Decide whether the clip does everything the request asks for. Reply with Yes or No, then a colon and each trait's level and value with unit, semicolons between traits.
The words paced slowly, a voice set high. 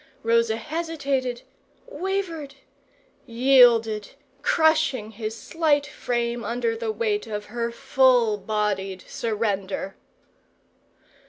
Yes: slow, 90 wpm; high, 235 Hz